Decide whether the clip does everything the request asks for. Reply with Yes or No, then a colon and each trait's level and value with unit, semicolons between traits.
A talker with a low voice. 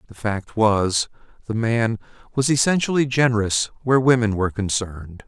Yes: low, 115 Hz